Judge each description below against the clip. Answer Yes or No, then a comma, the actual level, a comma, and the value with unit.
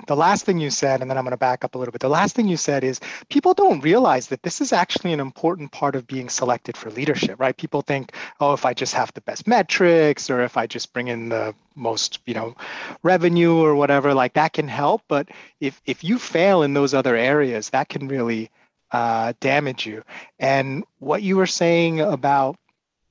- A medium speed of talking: No, fast, 220 wpm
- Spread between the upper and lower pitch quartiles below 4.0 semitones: No, average, 4.6 semitones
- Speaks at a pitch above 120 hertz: Yes, medium, 140 Hz